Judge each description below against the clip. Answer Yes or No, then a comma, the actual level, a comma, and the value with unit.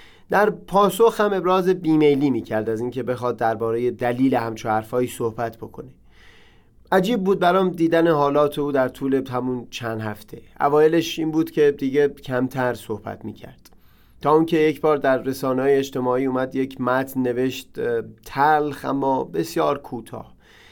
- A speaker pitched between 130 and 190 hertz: Yes, low, 135 Hz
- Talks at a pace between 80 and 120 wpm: No, average, 150 wpm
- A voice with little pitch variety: No, average, 4.1 semitones